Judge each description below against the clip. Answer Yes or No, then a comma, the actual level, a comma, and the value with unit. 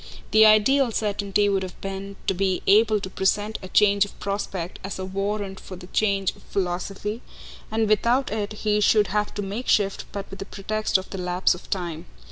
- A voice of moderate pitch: No, high, 200 Hz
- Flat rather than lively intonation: Yes, narrow, 1.8 semitones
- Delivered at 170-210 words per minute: Yes, average, 200 wpm